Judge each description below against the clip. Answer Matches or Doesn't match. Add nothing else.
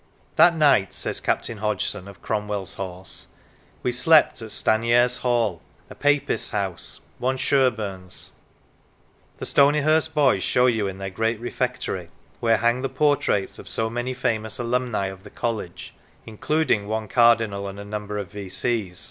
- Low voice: Matches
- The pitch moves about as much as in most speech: Matches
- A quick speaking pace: Doesn't match